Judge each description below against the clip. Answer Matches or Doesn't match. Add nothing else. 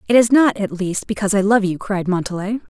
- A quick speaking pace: Matches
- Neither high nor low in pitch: Doesn't match